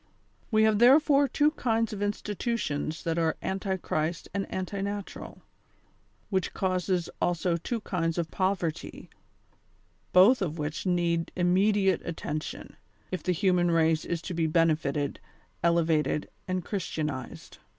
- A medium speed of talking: No, slow, 130 wpm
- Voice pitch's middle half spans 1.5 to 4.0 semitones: Yes, average, 3.5 semitones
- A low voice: No, medium, 180 Hz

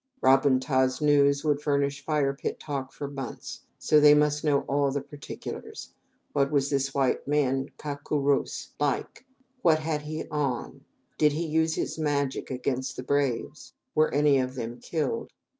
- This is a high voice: No, medium, 145 Hz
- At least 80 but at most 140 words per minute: No, average, 175 wpm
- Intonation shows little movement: Yes, narrow, 1.6 semitones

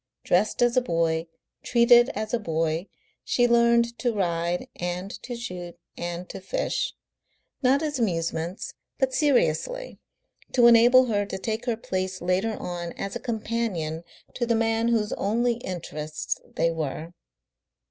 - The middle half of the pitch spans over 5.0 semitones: Yes, wide, 5.5 semitones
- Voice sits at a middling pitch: No, high, 215 Hz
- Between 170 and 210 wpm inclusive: No, average, 145 wpm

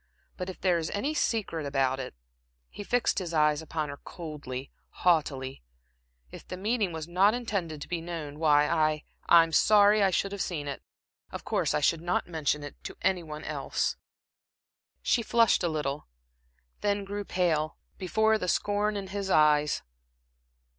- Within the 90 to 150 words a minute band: No, average, 165 wpm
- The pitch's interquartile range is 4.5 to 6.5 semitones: Yes, average, 4.9 semitones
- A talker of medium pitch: Yes, medium, 170 Hz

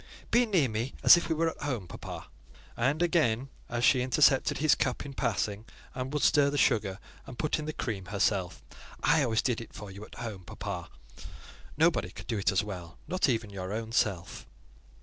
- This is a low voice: Yes, low, 120 Hz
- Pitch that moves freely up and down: Yes, wide, 5.8 semitones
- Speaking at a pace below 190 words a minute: No, average, 200 wpm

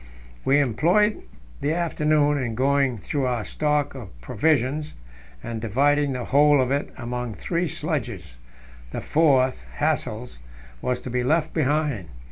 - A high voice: No, medium, 140 Hz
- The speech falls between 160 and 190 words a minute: No, slow, 135 wpm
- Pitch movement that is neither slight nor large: Yes, average, 3.4 semitones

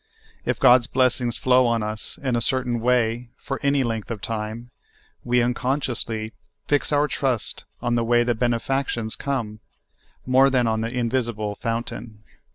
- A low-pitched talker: Yes, low, 120 Hz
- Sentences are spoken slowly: No, average, 160 wpm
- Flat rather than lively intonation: Yes, narrow, 2.1 semitones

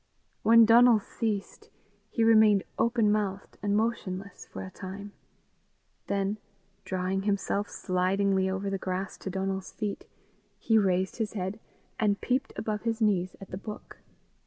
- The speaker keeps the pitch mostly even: Yes, narrow, 2.3 semitones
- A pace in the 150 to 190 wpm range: No, average, 140 wpm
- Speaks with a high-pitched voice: Yes, high, 200 Hz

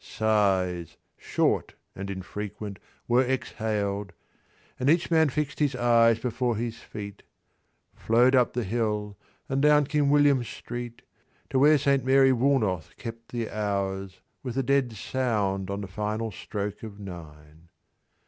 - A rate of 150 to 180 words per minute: No, average, 140 wpm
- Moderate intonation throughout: Yes, average, 4.6 semitones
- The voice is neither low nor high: No, low, 115 Hz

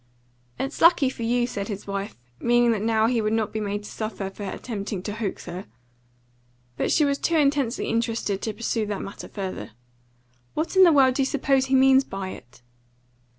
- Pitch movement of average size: Yes, average, 4.6 semitones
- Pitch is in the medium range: No, high, 225 Hz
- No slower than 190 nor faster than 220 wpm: Yes, average, 195 wpm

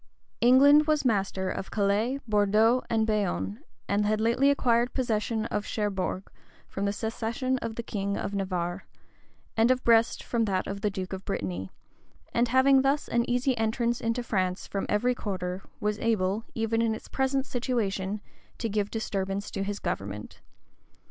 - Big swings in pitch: No, average, 3.3 semitones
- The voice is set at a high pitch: Yes, high, 220 Hz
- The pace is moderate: Yes, average, 160 wpm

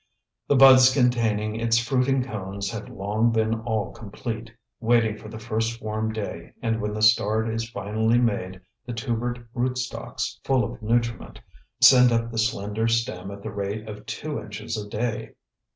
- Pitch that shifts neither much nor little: No, narrow, 1.8 semitones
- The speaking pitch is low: Yes, low, 115 Hz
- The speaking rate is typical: Yes, average, 165 wpm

